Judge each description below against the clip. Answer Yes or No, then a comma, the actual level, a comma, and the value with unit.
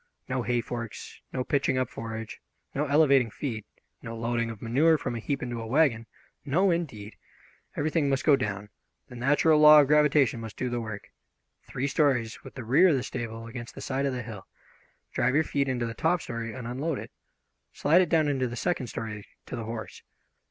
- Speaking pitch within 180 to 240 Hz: No, low, 125 Hz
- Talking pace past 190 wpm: Yes, average, 200 wpm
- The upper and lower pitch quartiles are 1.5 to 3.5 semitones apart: No, average, 4.1 semitones